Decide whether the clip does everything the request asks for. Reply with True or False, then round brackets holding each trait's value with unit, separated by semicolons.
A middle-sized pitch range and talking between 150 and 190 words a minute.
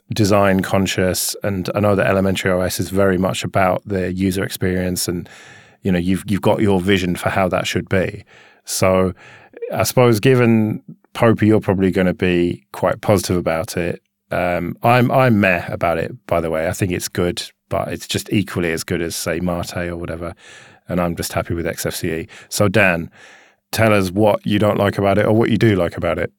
False (3.2 semitones; 200 wpm)